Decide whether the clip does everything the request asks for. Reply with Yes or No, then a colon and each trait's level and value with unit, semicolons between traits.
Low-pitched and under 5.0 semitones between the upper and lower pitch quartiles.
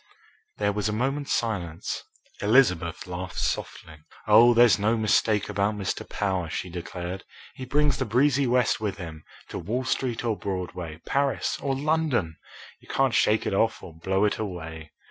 No: low, 105 Hz; wide, 5.4 semitones